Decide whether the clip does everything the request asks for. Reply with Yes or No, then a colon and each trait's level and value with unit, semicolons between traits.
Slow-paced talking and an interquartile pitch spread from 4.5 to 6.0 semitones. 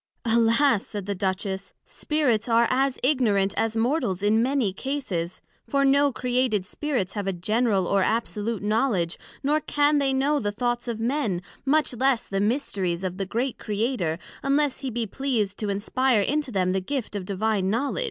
No: average, 170 wpm; average, 5.2 semitones